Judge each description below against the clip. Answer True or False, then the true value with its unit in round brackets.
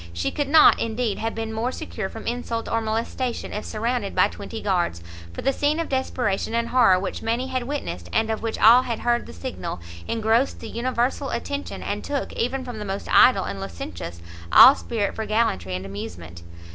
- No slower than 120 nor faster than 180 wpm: False (195 wpm)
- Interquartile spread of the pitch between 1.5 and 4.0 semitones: False (4.4 semitones)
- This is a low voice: False (225 Hz)